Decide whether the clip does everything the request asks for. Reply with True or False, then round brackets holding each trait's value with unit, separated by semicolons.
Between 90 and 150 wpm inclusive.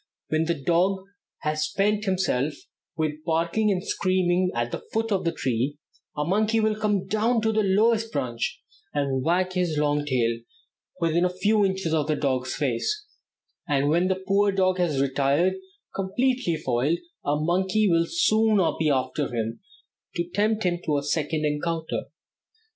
False (160 wpm)